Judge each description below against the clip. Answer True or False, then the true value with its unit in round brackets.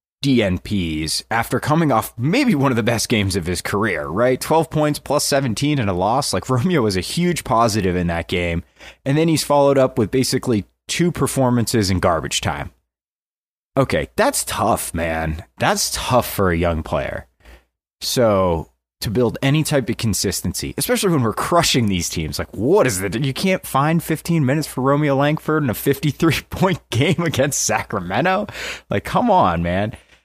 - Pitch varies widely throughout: True (7.5 semitones)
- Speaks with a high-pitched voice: False (125 Hz)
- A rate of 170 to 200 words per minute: True (175 wpm)